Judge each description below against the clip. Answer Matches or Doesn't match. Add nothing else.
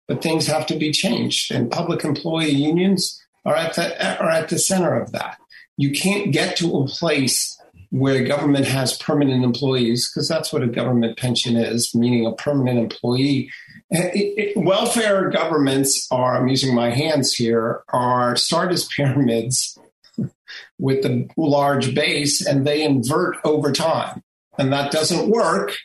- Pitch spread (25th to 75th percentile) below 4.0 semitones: Doesn't match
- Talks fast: Doesn't match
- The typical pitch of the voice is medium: Matches